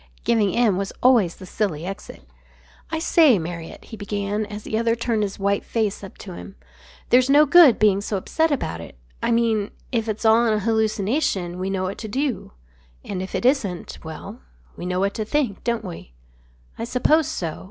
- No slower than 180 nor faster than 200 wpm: Yes, average, 195 wpm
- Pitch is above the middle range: Yes, high, 215 Hz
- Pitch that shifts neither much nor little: Yes, average, 3.5 semitones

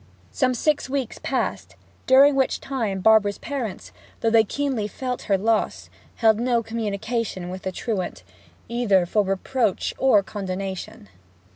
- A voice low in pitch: No, high, 220 Hz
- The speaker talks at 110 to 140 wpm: Yes, slow, 135 wpm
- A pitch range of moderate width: Yes, average, 4.3 semitones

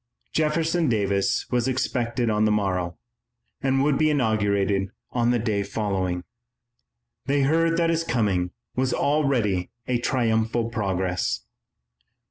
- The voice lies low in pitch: Yes, low, 115 Hz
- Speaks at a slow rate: Yes, slow, 120 wpm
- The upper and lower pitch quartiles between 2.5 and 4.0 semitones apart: No, average, 5.2 semitones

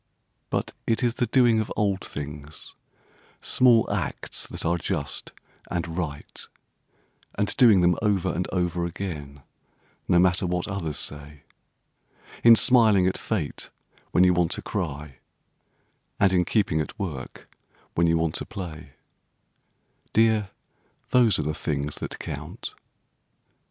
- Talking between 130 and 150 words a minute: Yes, slow, 135 wpm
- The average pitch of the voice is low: Yes, very low, 90 Hz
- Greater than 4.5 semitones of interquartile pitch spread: Yes, average, 5.1 semitones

